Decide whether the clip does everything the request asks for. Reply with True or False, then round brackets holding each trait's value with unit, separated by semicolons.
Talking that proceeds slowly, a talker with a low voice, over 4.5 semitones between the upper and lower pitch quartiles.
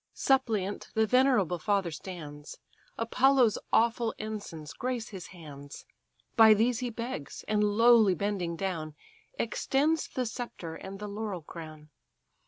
False (125 wpm; 210 Hz; 5.5 semitones)